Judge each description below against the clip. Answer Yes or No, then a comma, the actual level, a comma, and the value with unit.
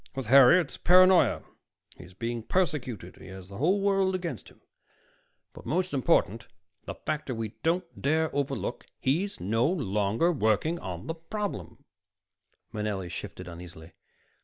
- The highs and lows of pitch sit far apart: Yes, wide, 9.0 semitones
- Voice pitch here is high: No, low, 135 Hz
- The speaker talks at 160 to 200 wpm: No, slow, 135 wpm